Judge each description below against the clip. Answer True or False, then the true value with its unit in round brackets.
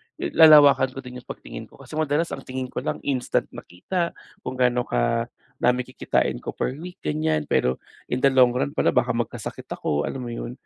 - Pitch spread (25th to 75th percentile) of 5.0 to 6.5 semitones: False (3.0 semitones)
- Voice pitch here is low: True (130 Hz)